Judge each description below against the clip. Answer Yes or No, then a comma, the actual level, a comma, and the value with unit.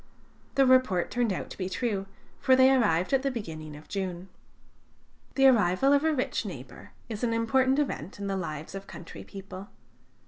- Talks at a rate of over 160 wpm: Yes, average, 180 wpm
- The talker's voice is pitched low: No, high, 210 Hz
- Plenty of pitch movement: Yes, wide, 6.0 semitones